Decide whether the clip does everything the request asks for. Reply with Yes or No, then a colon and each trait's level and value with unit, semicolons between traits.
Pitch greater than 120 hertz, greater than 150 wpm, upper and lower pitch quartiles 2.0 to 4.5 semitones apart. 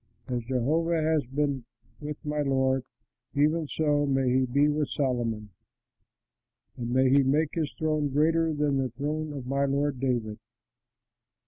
No: medium, 140 Hz; average, 145 wpm; narrow, 2.4 semitones